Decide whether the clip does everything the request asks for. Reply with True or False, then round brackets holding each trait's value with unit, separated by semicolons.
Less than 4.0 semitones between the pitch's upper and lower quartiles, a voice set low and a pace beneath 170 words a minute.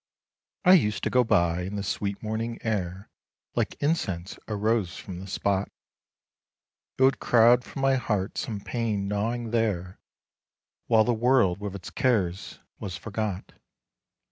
True (3.6 semitones; 105 Hz; 145 wpm)